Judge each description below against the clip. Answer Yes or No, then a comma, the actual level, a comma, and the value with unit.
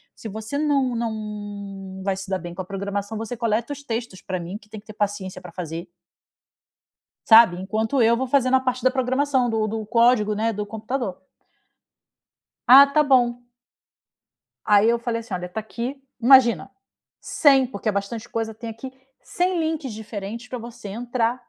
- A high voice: Yes, high, 225 Hz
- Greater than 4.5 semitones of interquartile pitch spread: No, average, 3.7 semitones